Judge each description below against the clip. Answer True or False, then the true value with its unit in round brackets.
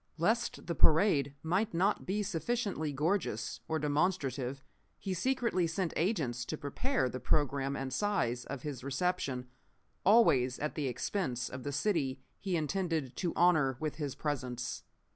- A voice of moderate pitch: True (155 Hz)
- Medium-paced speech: True (145 wpm)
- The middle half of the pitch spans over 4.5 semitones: True (5.6 semitones)